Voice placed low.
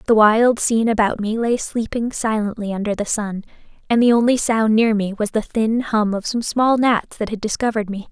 No: high, 220 Hz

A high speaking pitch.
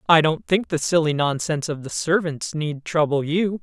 No: medium, 160 Hz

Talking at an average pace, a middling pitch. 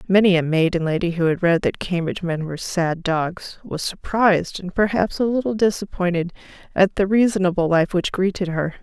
Yes: average, 185 wpm; medium, 180 Hz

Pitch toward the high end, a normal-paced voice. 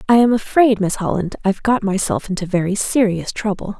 Yes: high, 205 Hz; average, 190 wpm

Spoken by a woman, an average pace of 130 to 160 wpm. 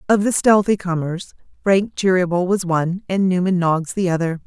No: female; average, 175 wpm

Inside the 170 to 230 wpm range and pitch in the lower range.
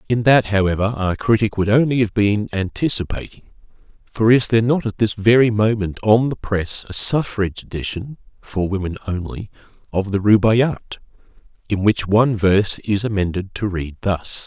No: average, 160 wpm; low, 105 Hz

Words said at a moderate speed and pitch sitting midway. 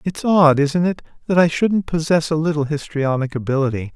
Yes: average, 180 wpm; medium, 155 Hz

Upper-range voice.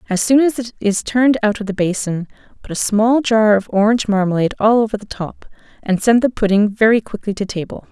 Yes: high, 215 Hz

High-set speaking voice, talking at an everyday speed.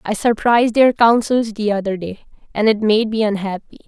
Yes: high, 215 Hz; average, 185 wpm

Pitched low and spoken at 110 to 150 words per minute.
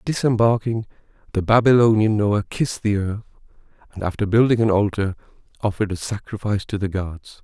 Yes: low, 105 Hz; average, 145 wpm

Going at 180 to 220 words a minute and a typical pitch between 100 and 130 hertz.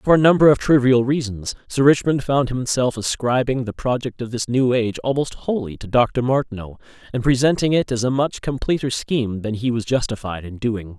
Yes: average, 195 wpm; low, 125 Hz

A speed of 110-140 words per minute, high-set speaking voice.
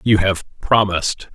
No: slow, 135 wpm; low, 100 Hz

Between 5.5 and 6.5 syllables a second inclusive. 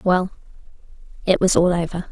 Yes: 5.6 syllables/s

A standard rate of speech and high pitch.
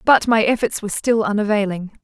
Yes: average, 175 wpm; high, 215 Hz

